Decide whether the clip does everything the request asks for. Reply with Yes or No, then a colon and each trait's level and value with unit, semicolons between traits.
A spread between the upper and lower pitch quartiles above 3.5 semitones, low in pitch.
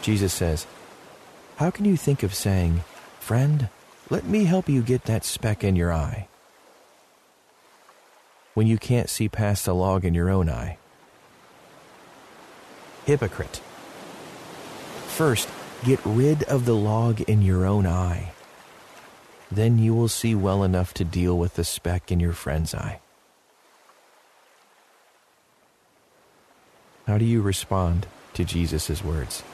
Yes: average, 4.6 semitones; low, 100 Hz